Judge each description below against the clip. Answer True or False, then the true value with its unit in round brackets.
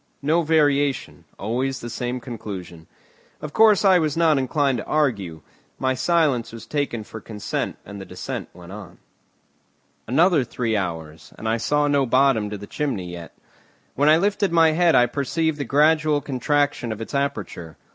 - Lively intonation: True (6.0 semitones)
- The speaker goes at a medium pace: True (165 wpm)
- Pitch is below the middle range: True (130 Hz)